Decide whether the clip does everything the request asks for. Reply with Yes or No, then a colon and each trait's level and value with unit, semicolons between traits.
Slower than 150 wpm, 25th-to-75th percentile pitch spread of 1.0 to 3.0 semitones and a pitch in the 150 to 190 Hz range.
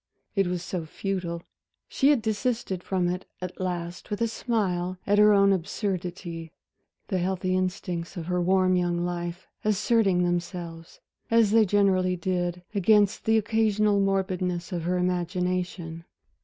Yes: average, 140 wpm; narrow, 2.5 semitones; medium, 185 Hz